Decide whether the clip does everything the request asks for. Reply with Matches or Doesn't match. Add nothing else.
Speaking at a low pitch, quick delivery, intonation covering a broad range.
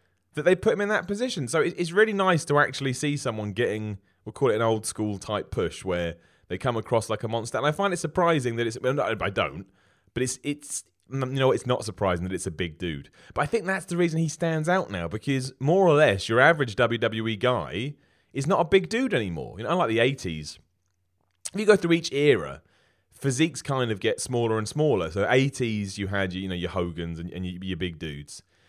Matches